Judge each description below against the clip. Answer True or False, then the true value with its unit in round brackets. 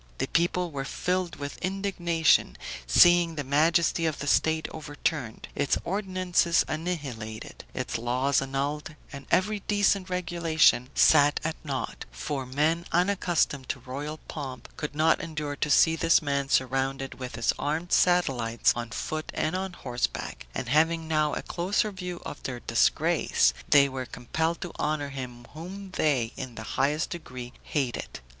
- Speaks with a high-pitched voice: False (150 Hz)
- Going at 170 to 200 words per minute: False (150 wpm)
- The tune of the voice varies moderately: True (4.3 semitones)